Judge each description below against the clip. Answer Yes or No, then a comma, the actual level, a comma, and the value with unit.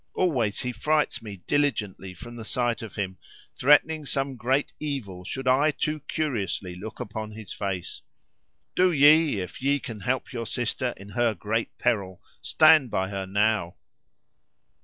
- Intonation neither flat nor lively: No, wide, 5.8 semitones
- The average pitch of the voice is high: No, low, 115 Hz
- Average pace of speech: Yes, average, 155 wpm